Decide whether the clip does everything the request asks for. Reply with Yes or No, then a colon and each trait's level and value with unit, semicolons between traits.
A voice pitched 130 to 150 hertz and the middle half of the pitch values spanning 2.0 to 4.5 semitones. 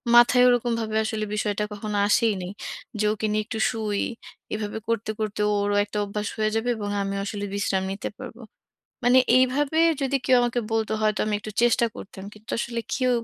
No: high, 215 Hz; narrow, 2.6 semitones